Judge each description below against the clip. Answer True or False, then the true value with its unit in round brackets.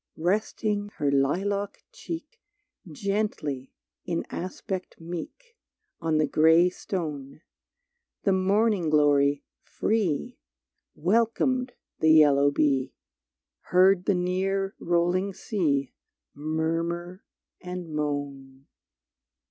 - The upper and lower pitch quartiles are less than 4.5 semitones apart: False (4.8 semitones)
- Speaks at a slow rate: True (85 wpm)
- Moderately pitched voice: True (175 Hz)